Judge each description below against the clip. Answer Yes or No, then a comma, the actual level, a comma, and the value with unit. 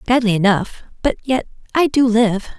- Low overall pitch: No, high, 230 Hz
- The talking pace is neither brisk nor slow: Yes, average, 160 wpm